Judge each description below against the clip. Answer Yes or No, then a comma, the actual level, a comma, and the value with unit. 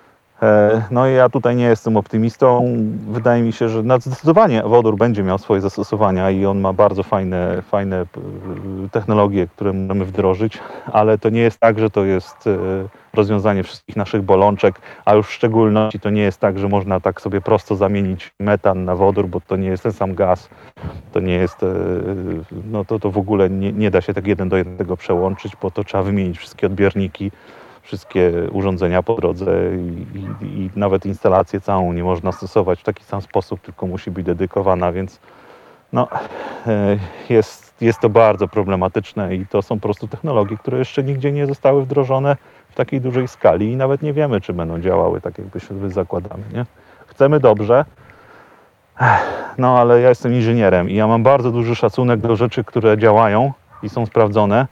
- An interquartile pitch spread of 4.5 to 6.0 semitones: No, average, 3.2 semitones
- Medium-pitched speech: No, low, 105 Hz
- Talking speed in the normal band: No, fast, 180 wpm